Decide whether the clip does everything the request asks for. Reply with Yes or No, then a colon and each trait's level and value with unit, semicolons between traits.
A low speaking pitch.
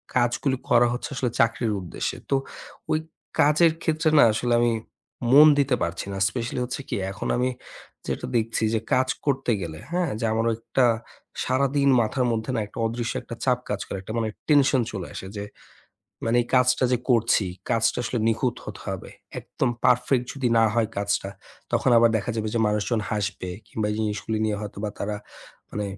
Yes: low, 120 Hz